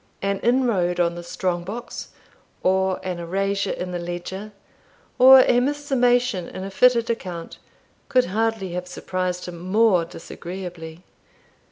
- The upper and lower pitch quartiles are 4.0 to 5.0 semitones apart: Yes, average, 4.6 semitones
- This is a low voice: No, high, 190 Hz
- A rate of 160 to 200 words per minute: No, average, 140 wpm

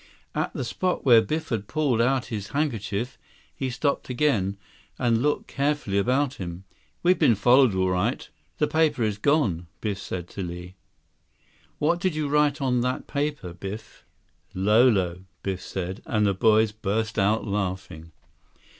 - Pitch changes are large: Yes, wide, 6.3 semitones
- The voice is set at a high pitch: No, low, 110 Hz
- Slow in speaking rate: No, average, 155 wpm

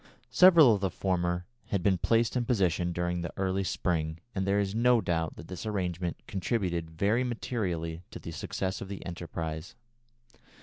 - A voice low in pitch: Yes, very low, 95 Hz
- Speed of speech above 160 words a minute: Yes, average, 170 wpm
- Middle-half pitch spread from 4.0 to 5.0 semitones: No, average, 3.3 semitones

